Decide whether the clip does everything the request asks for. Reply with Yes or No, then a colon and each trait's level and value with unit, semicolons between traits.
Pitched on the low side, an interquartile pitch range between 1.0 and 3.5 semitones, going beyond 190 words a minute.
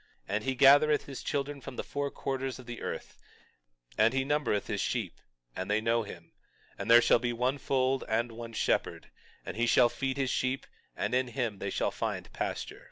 Yes: low, 125 Hz; average, 2.8 semitones; fast, 205 wpm